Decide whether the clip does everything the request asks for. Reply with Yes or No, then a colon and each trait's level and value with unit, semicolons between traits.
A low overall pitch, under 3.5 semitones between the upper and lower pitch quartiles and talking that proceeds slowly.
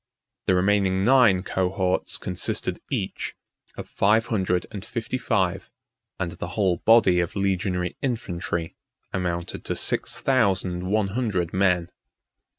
Yes: very low, 95 Hz; narrow, 2.6 semitones; slow, 125 wpm